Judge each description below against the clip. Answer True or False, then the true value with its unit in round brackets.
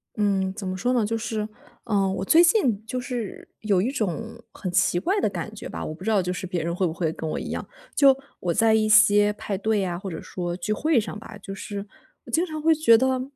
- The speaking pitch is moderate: False (210 Hz)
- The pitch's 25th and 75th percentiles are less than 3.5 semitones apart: False (3.8 semitones)